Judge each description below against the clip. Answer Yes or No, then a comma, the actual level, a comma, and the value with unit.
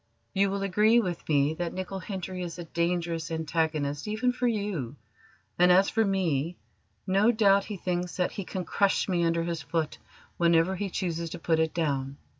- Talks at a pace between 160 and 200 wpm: Yes, average, 185 wpm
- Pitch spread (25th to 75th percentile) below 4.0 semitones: Yes, average, 3.1 semitones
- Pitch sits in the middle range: Yes, medium, 175 Hz